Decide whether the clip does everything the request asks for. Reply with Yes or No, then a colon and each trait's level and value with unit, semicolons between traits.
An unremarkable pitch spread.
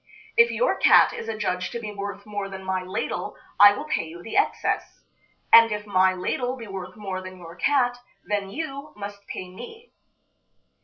Yes: average, 4.0 semitones